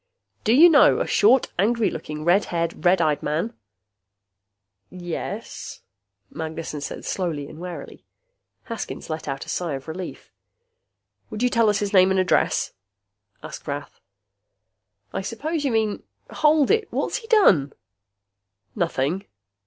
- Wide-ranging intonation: Yes, wide, 6.4 semitones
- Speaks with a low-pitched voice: No, medium, 185 Hz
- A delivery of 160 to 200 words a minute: No, slow, 135 wpm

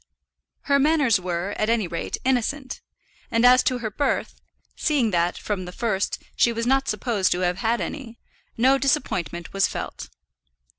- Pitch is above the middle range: Yes, high, 230 Hz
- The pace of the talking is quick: No, average, 160 wpm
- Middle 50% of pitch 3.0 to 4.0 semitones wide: No, wide, 5.6 semitones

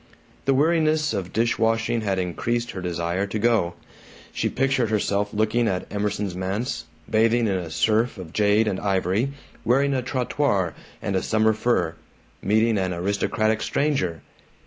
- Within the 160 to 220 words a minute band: No, average, 150 wpm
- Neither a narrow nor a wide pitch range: Yes, average, 3.8 semitones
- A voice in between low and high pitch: No, low, 110 Hz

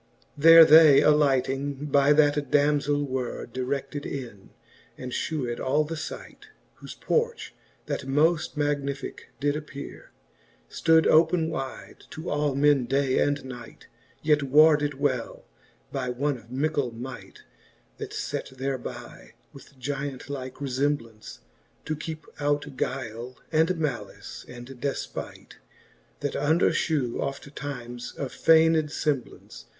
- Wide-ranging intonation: No, narrow, 2.4 semitones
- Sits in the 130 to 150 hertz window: Yes, medium, 140 Hz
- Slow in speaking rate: Yes, slow, 125 wpm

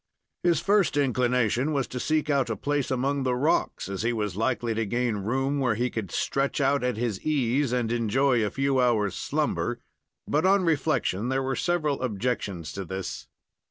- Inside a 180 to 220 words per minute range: Yes, average, 185 wpm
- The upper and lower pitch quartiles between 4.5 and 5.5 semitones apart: No, average, 3.7 semitones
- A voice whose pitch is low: Yes, low, 125 Hz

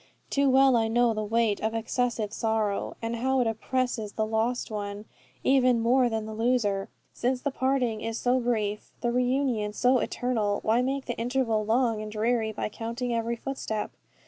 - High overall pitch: Yes, high, 230 Hz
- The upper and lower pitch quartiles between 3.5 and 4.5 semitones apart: No, narrow, 2.4 semitones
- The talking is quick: No, average, 175 wpm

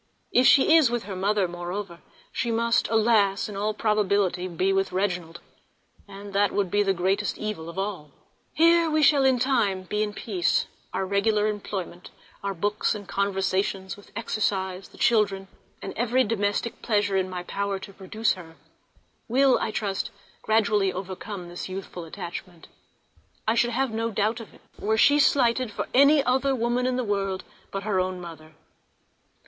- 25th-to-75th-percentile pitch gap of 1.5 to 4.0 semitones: Yes, average, 3.2 semitones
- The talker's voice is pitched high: Yes, high, 205 Hz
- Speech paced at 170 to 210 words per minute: Yes, average, 175 wpm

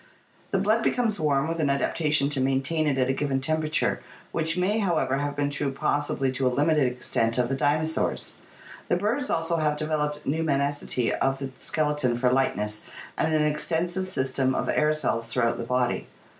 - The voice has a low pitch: No, medium, 145 Hz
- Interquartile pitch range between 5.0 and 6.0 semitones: No, average, 3.1 semitones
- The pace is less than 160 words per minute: No, average, 185 wpm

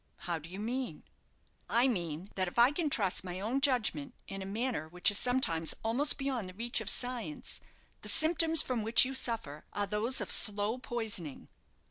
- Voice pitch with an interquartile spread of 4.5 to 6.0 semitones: Yes, average, 5.2 semitones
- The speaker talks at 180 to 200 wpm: Yes, average, 185 wpm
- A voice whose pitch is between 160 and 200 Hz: No, high, 230 Hz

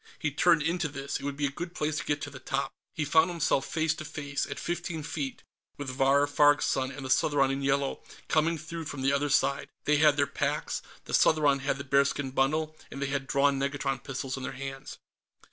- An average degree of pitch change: No, narrow, 2.2 semitones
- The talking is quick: Yes, fast, 225 wpm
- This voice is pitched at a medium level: Yes, medium, 145 Hz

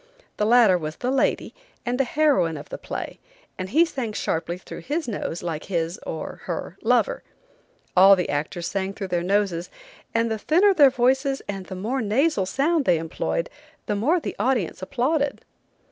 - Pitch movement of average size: No, wide, 7.0 semitones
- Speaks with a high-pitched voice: Yes, high, 210 Hz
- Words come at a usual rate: Yes, average, 175 wpm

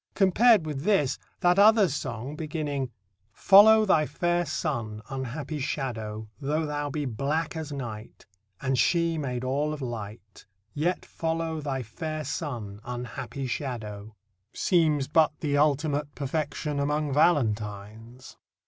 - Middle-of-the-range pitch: Yes, medium, 145 Hz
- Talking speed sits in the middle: No, slow, 125 wpm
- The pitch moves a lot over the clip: No, average, 4.3 semitones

